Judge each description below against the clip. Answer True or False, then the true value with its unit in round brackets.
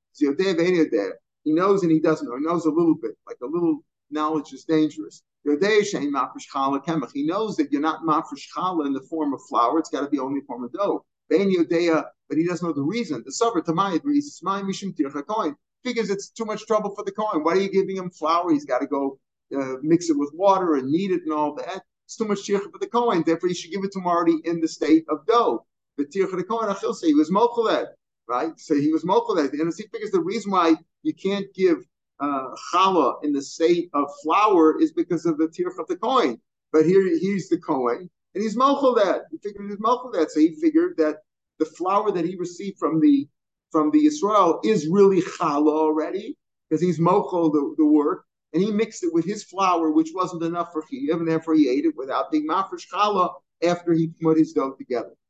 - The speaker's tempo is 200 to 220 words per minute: True (205 wpm)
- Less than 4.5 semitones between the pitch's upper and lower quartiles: False (5.0 semitones)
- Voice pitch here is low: False (175 Hz)